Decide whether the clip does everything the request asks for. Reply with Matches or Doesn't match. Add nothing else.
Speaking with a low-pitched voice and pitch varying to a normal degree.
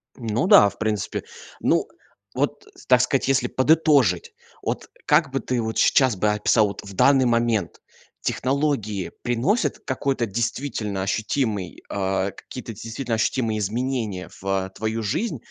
Matches